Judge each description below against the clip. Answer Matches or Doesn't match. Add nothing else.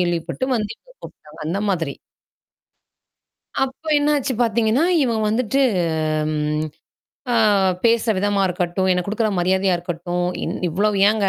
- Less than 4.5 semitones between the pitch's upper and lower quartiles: Doesn't match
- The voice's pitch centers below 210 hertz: Matches